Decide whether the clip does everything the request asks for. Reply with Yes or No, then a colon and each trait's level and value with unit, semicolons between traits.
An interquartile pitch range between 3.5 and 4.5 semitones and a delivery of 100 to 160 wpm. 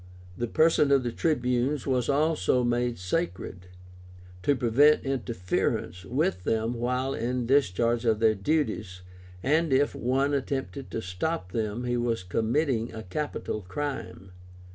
Yes: average, 4.1 semitones; average, 140 wpm